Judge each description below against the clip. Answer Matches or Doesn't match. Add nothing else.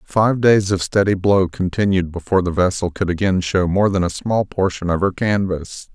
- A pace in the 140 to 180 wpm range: Doesn't match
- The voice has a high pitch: Doesn't match